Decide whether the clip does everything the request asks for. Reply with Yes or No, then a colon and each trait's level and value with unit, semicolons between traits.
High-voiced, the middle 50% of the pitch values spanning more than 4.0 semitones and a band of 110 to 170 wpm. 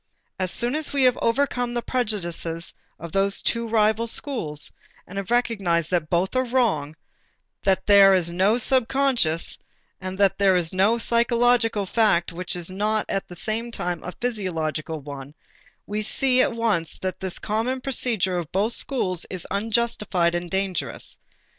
Yes: high, 200 Hz; average, 4.9 semitones; average, 160 wpm